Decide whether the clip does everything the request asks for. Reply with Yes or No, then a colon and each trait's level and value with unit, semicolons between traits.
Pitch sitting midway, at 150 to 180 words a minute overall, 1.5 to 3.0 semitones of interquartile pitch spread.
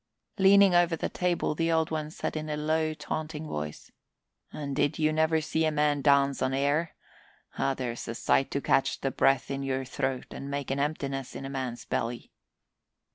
No: medium, 145 Hz; average, 190 wpm; narrow, 2.6 semitones